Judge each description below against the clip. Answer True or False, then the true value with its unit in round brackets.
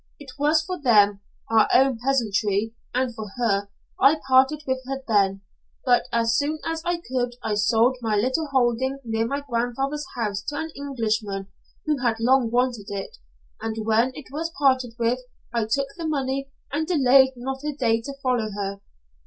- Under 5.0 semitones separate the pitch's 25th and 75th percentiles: True (3.6 semitones)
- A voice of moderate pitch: False (250 Hz)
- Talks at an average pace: True (175 wpm)